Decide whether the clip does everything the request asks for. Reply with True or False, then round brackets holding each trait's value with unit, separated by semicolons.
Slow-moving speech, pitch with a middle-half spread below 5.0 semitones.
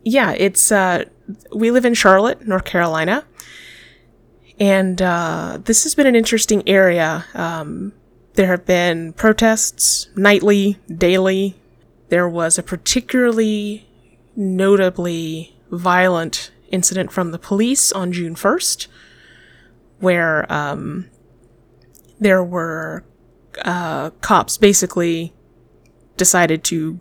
True (100 wpm; 3.4 semitones)